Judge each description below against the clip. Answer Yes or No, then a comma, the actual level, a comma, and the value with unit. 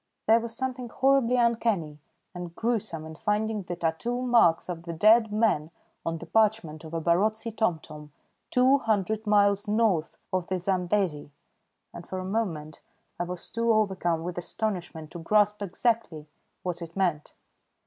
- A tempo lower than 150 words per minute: No, average, 155 wpm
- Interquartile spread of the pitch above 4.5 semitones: Yes, average, 4.9 semitones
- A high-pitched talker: Yes, high, 195 Hz